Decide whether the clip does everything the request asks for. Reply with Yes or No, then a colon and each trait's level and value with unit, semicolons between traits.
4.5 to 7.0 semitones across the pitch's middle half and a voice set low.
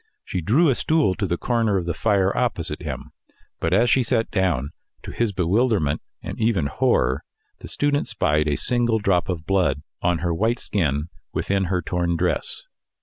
Yes: average, 5.3 semitones; very low, 95 Hz